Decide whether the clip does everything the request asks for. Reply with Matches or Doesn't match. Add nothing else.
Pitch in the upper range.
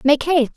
Matches